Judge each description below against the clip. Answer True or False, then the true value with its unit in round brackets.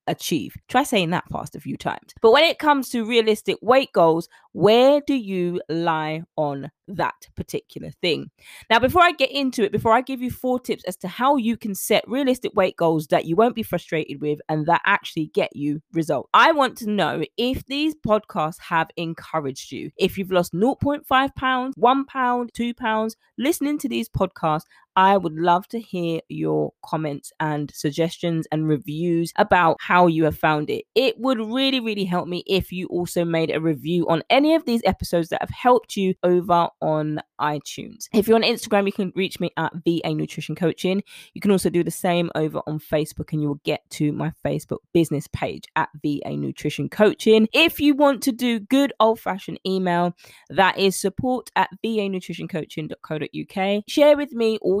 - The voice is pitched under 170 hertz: False (190 Hz)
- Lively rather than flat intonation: True (6.5 semitones)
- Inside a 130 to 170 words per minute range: False (190 wpm)